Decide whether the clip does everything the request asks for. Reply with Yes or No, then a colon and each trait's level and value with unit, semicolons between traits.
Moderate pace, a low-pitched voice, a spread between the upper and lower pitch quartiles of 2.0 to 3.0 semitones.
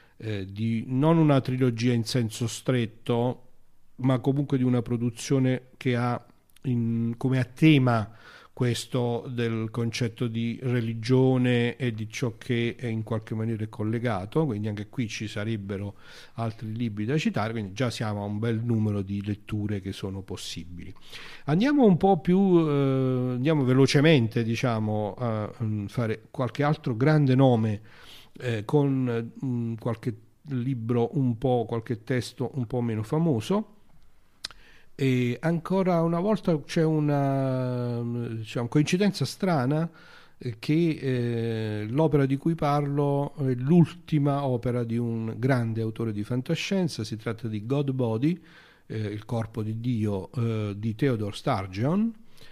No: average, 135 wpm; low, 125 Hz; average, 3.8 semitones